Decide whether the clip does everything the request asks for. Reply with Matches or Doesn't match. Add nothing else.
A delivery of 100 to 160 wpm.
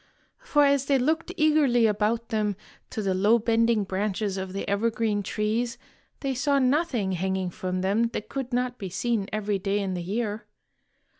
Doesn't match